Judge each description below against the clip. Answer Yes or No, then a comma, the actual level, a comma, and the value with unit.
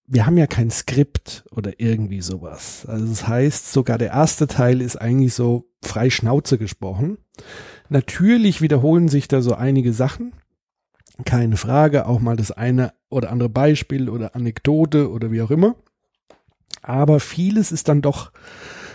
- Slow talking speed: No, average, 150 wpm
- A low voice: Yes, low, 125 Hz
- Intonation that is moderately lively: Yes, average, 4.0 semitones